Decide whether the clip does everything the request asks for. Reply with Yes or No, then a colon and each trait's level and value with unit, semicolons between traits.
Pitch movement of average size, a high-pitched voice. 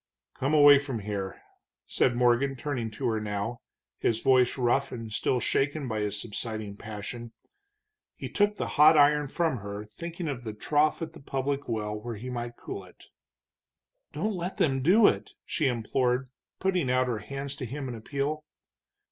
No: average, 4.5 semitones; low, 130 Hz